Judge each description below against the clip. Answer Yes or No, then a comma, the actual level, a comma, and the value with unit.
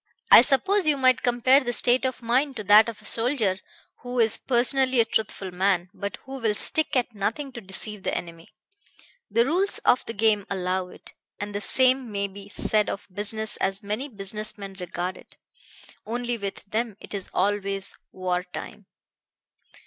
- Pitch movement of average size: Yes, average, 4.1 semitones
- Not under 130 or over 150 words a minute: No, average, 180 wpm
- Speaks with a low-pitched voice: No, high, 215 Hz